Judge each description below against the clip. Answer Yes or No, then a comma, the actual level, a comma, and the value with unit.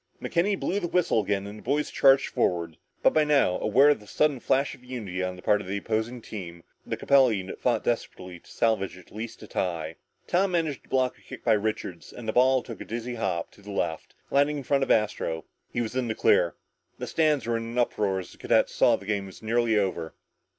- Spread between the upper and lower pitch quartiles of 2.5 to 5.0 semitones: No, wide, 5.4 semitones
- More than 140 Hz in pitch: No, low, 110 Hz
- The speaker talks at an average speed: No, fast, 240 wpm